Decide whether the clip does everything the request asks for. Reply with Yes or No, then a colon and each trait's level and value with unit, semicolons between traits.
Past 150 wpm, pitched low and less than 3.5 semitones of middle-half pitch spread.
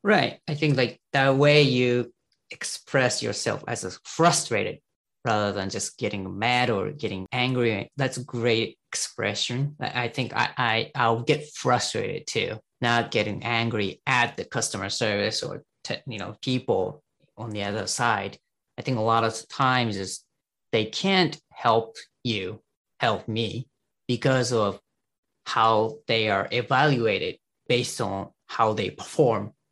No: average, 145 wpm; low, 120 Hz; average, 2.9 semitones